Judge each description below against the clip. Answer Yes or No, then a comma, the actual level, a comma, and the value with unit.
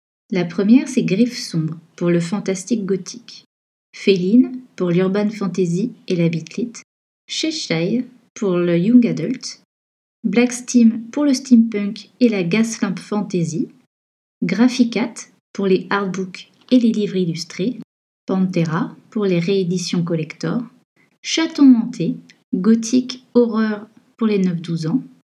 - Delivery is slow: Yes, slow, 120 wpm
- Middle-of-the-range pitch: No, high, 215 Hz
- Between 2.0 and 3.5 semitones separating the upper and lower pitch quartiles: No, average, 4.6 semitones